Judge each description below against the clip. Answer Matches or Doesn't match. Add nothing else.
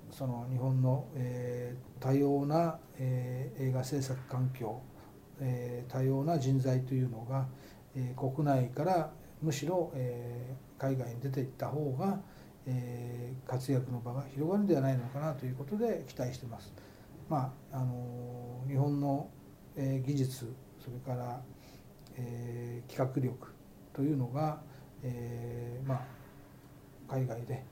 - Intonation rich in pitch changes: Doesn't match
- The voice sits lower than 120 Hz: Doesn't match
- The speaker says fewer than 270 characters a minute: Matches